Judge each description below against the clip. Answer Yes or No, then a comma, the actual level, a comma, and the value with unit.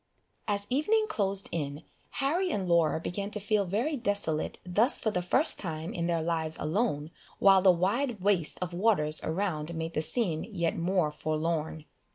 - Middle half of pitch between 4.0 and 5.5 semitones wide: Yes, average, 4.5 semitones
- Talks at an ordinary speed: Yes, average, 170 wpm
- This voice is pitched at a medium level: Yes, medium, 180 Hz